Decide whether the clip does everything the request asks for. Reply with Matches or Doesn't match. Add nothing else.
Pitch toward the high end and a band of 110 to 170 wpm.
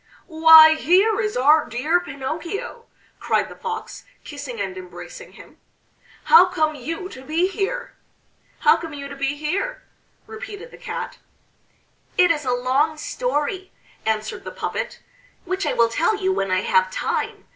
Matches